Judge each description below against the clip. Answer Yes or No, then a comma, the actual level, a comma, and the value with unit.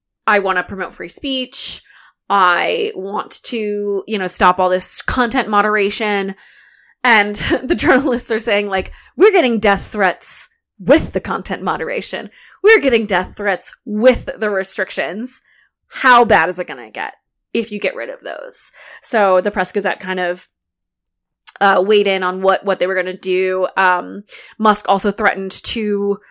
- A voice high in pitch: Yes, high, 200 Hz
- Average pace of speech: Yes, average, 165 wpm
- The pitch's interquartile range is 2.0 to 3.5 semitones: Yes, average, 3.1 semitones